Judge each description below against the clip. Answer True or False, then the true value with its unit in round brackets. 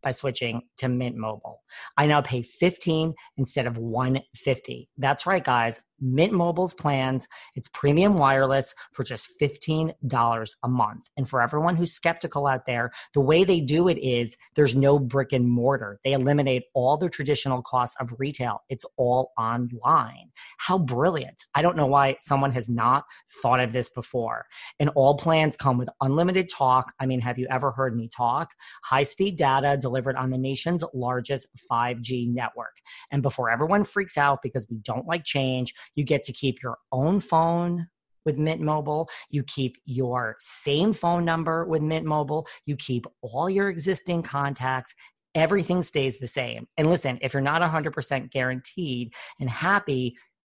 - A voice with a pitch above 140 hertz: False (135 Hz)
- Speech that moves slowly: False (165 wpm)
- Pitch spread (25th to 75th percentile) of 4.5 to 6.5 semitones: False (3.8 semitones)